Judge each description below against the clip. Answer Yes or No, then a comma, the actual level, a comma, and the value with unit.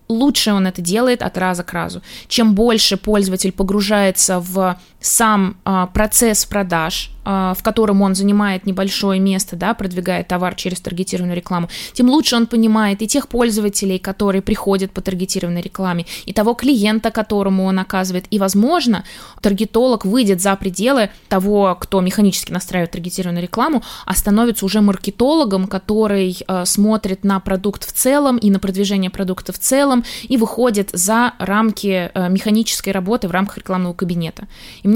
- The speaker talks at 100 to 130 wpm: No, average, 155 wpm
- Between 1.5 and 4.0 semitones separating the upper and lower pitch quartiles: Yes, average, 2.8 semitones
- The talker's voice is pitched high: Yes, high, 200 Hz